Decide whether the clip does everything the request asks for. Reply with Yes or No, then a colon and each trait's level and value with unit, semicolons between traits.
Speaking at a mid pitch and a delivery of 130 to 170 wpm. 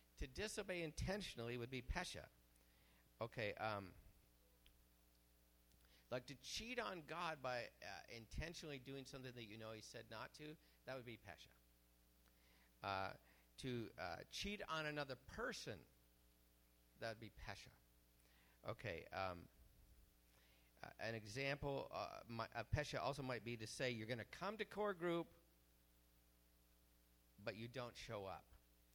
No: low, 110 Hz; slow, 135 wpm